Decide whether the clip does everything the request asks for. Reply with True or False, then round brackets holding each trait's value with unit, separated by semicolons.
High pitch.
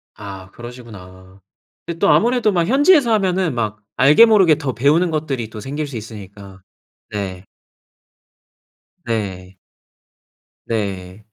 False (120 Hz)